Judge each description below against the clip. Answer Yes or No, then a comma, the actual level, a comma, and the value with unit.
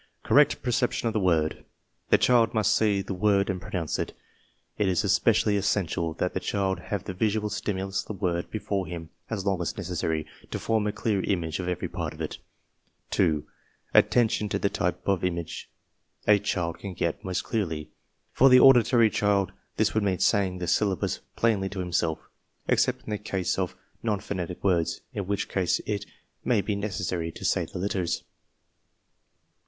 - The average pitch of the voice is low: Yes, very low, 95 Hz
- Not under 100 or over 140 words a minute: No, average, 180 wpm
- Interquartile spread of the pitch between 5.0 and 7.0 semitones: No, average, 2.8 semitones